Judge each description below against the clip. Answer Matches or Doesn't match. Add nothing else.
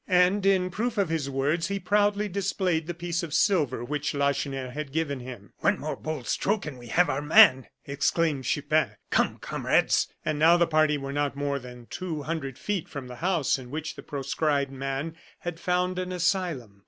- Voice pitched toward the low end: Doesn't match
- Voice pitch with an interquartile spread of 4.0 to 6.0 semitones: Matches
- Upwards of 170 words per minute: Matches